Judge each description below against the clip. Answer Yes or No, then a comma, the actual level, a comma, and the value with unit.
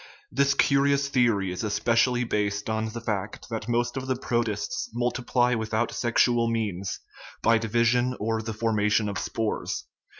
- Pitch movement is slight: Yes, narrow, 2.2 semitones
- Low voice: Yes, low, 115 Hz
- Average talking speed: Yes, average, 145 wpm